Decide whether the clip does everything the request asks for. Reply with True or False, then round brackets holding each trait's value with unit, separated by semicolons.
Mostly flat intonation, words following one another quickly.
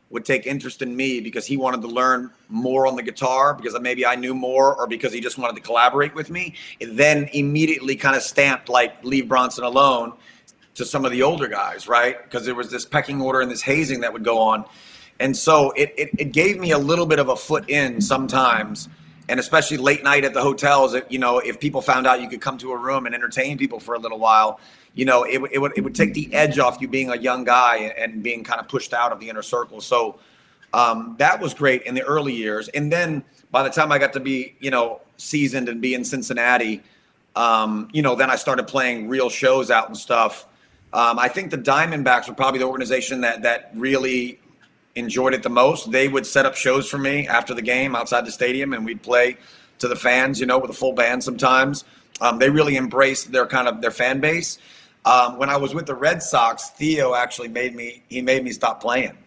True (2.1 semitones; 235 wpm)